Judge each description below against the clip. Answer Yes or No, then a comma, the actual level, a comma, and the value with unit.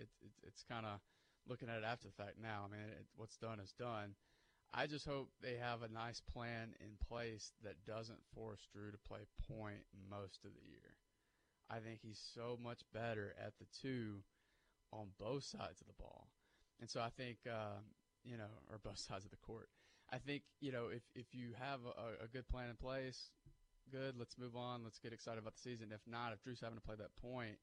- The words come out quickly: Yes, fast, 220 wpm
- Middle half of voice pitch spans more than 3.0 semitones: No, average, 2.7 semitones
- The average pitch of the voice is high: No, low, 115 Hz